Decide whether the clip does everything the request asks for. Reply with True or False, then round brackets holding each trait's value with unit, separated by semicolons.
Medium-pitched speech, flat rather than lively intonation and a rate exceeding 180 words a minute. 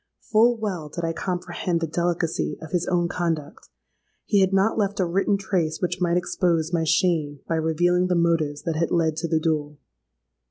True (170 Hz; 2.2 semitones; 190 wpm)